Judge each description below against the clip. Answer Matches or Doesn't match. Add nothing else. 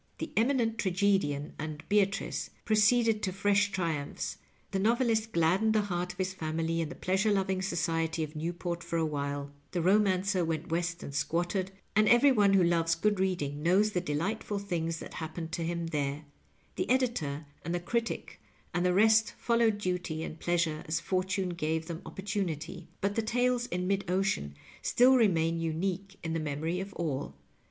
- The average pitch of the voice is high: Doesn't match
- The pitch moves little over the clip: Doesn't match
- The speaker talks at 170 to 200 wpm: Matches